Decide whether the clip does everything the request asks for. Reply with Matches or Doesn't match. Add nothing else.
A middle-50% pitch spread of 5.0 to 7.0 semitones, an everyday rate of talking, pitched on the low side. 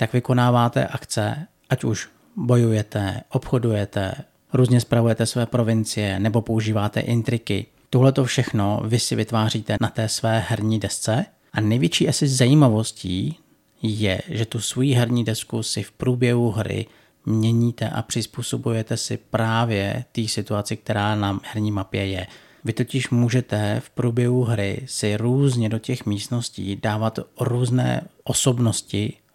Doesn't match